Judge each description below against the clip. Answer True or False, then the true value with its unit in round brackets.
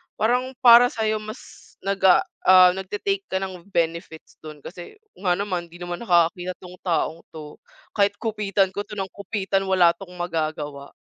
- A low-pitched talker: False (185 Hz)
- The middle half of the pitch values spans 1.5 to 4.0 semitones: True (2.9 semitones)